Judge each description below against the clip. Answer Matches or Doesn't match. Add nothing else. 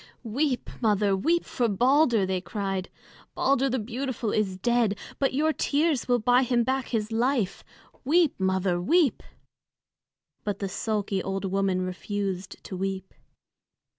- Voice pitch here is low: Doesn't match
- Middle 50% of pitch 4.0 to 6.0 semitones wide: Matches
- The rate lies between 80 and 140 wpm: Matches